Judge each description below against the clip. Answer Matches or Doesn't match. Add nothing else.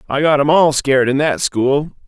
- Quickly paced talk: Matches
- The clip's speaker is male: Matches